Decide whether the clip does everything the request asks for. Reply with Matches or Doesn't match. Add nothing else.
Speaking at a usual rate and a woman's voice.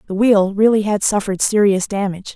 Matches